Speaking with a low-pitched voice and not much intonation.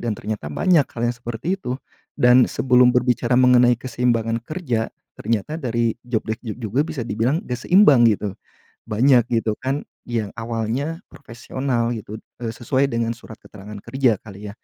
Yes: low, 120 Hz; narrow, 2.3 semitones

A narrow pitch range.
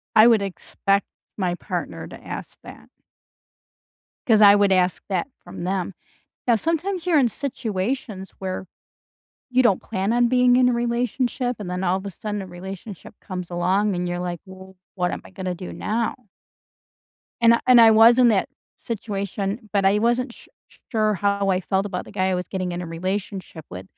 No: average, 4.0 semitones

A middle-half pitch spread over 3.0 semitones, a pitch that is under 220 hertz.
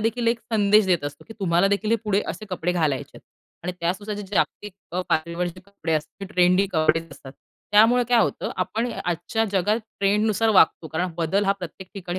Yes: average, 3.6 semitones; high, 190 Hz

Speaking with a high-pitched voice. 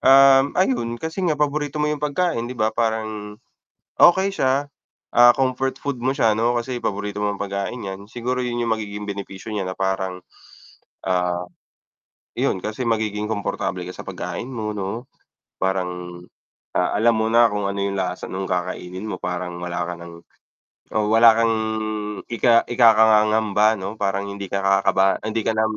No: low, 110 Hz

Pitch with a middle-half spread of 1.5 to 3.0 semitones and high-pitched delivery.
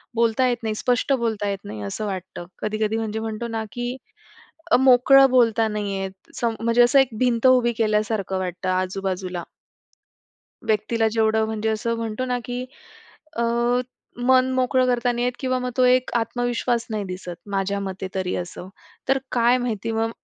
No: average, 3.4 semitones; high, 225 Hz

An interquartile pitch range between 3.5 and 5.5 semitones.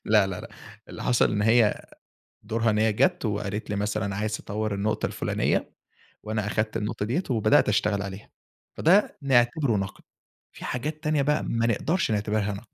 No: average, 2.8 semitones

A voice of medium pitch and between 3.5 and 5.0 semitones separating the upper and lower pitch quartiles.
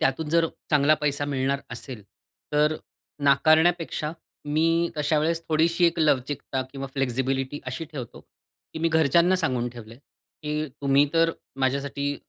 No: medium, 150 Hz; average, 3.1 semitones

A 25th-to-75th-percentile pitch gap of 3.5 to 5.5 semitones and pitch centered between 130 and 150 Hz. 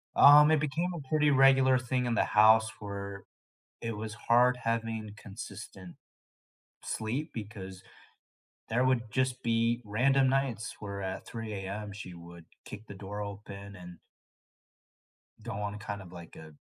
No: average, 4.2 semitones; low, 110 Hz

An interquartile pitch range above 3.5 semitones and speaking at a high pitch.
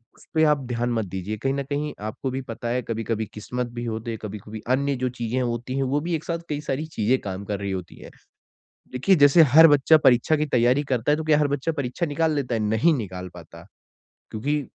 No: average, 4.8 semitones; low, 125 Hz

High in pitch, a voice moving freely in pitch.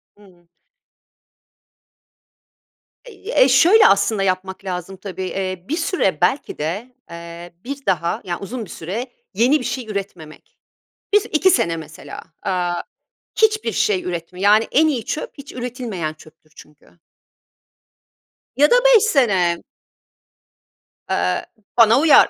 Yes: high, 195 Hz; wide, 6.7 semitones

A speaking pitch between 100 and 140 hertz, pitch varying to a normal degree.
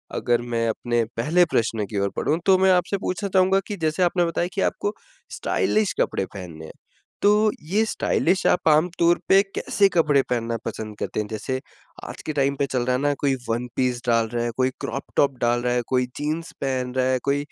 No: low, 135 Hz; wide, 6.7 semitones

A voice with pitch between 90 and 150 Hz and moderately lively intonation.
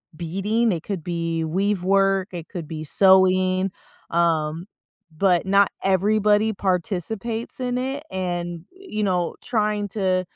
No: high, 190 Hz; average, 3.1 semitones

